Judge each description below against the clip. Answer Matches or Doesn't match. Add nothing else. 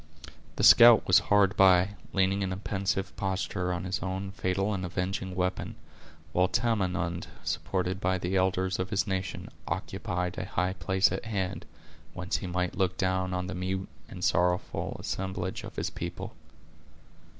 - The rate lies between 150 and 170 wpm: Matches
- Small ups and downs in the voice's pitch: Matches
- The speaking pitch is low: Matches